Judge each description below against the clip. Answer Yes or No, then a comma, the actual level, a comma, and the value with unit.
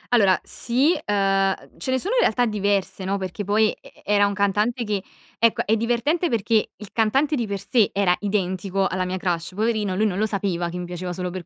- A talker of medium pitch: No, high, 205 Hz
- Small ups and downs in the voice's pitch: No, average, 3.3 semitones